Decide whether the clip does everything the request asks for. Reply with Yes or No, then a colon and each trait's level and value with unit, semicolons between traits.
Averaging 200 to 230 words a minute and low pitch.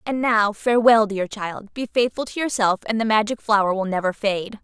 No: fast, 205 wpm; high, 215 Hz